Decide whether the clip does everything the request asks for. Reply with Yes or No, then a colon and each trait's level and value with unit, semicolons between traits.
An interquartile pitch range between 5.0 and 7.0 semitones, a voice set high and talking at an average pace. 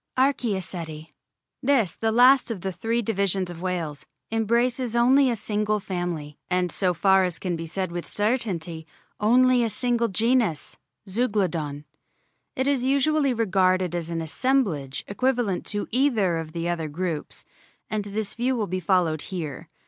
Yes: wide, 5.6 semitones; high, 195 Hz; average, 150 wpm